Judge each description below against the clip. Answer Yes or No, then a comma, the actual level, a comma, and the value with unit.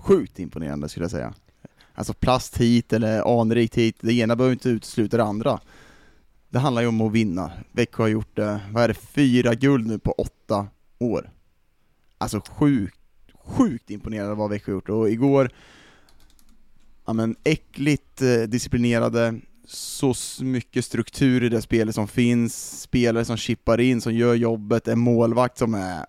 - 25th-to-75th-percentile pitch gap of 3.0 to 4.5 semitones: No, narrow, 2.4 semitones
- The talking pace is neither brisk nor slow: Yes, average, 160 wpm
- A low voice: Yes, low, 115 Hz